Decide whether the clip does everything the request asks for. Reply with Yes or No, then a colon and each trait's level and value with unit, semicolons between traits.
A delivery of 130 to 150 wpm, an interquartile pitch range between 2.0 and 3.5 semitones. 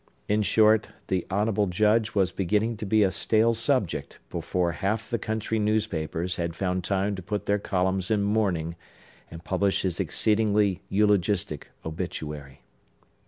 Yes: average, 145 wpm; average, 2.9 semitones